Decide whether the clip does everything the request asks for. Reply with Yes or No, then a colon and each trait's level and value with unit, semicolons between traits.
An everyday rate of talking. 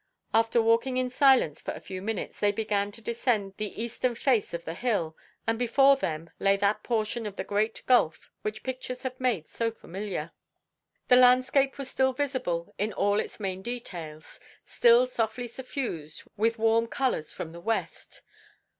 Yes: average, 170 wpm